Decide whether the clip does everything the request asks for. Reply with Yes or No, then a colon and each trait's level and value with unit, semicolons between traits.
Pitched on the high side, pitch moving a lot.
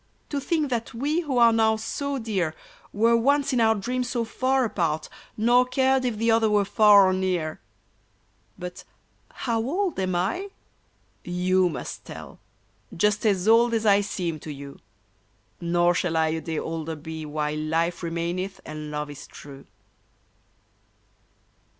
Yes: high, 200 Hz; wide, 6.0 semitones